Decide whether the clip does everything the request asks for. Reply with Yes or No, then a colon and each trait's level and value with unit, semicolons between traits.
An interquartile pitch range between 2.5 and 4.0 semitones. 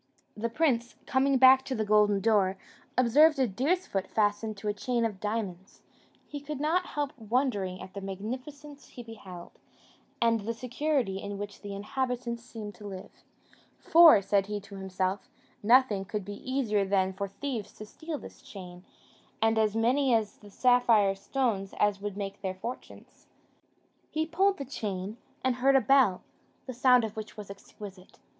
No: average, 4.6 semitones